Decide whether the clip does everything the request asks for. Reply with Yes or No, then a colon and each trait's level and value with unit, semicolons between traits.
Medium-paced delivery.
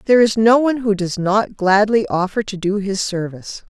No: fast, 210 wpm